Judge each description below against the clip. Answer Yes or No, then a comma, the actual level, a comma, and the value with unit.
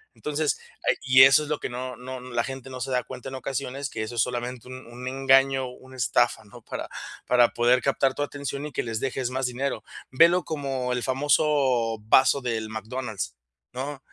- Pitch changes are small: Yes, narrow, 1.7 semitones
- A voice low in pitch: Yes, low, 130 Hz